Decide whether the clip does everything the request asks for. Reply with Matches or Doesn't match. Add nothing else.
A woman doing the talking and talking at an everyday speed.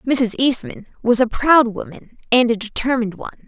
Matches